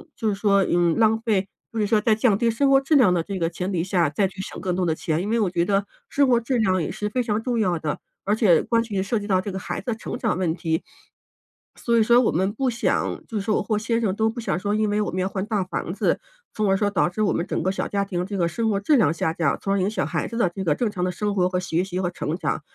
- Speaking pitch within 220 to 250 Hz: No, high, 200 Hz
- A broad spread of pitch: No, average, 3.4 semitones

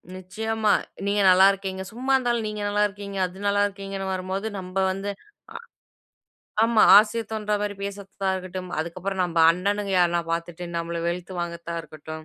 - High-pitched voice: Yes, high, 195 Hz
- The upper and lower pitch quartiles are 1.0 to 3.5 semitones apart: Yes, narrow, 2.5 semitones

